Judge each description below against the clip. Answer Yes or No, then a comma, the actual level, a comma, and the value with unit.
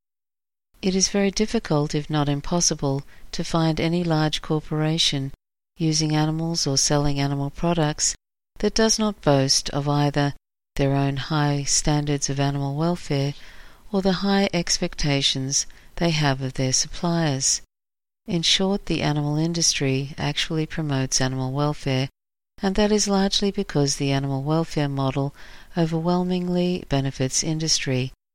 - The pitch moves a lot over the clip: No, average, 3.7 semitones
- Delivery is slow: Yes, slow, 130 wpm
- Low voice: No, medium, 150 Hz